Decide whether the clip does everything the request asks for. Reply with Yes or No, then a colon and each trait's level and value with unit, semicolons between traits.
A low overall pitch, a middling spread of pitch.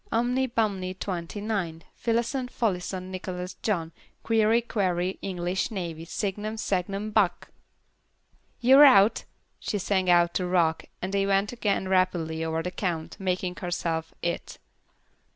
No: high, 190 Hz; average, 3.3 semitones